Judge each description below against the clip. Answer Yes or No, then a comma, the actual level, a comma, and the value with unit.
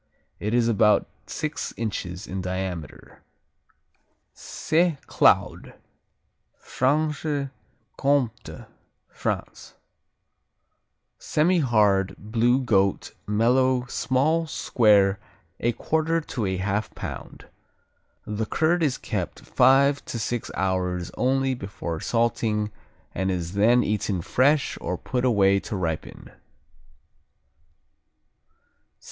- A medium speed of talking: No, slow, 95 wpm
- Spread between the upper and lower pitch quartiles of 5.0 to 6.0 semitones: Yes, wide, 5.6 semitones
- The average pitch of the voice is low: Yes, low, 115 Hz